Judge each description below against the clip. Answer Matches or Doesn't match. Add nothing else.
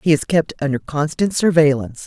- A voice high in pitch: Doesn't match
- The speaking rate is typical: Matches